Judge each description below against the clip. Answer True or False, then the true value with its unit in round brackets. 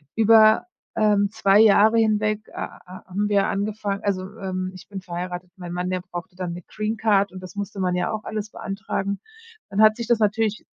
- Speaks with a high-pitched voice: True (200 Hz)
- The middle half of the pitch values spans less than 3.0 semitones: True (2.6 semitones)